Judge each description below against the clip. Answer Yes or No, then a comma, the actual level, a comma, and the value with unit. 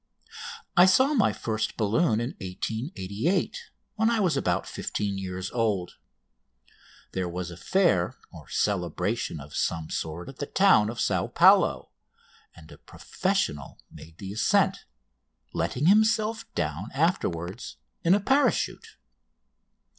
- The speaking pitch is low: Yes, low, 110 Hz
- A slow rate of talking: Yes, slow, 125 wpm